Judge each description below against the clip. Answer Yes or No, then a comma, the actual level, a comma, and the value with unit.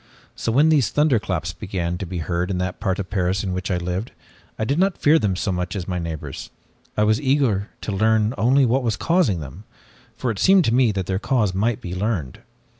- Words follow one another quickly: Yes, fast, 225 wpm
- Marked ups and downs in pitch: No, average, 5.0 semitones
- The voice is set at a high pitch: No, low, 100 Hz